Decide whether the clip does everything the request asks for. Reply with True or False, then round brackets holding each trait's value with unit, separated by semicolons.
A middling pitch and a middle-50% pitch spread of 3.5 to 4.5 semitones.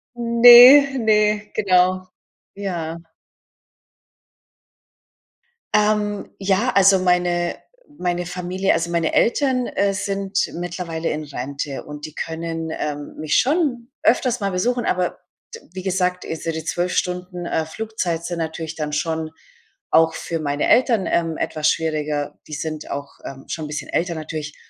True (175 Hz; 4.0 semitones)